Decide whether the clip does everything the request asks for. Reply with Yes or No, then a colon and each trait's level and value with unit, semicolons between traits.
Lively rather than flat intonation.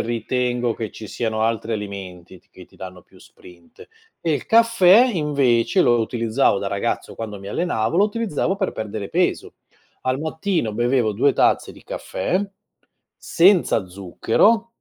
Yes: wide, 8.1 semitones